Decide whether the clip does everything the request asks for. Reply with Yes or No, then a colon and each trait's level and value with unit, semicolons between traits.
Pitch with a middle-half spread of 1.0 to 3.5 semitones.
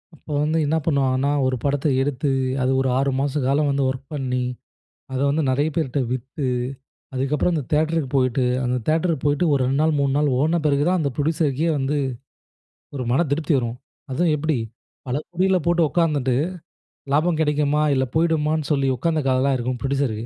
Yes: average, 3.0 semitones